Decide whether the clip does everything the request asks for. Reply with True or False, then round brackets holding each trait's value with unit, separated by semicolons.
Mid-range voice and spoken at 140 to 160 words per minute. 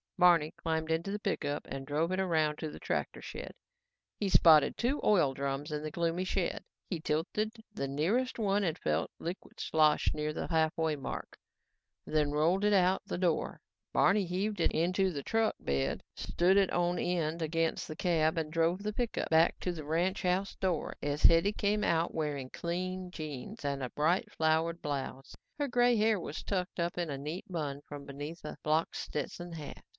False (165 Hz; 180 wpm)